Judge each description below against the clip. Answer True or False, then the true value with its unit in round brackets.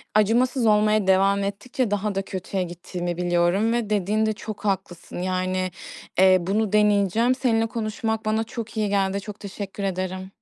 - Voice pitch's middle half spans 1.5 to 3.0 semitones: True (2.6 semitones)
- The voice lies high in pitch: True (200 Hz)